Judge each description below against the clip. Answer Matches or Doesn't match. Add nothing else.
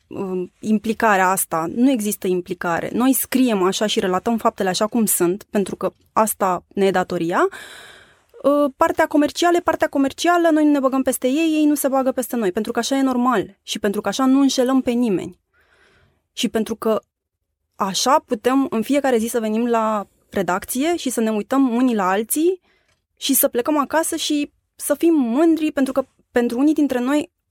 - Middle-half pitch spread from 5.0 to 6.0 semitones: Matches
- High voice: Matches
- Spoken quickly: Matches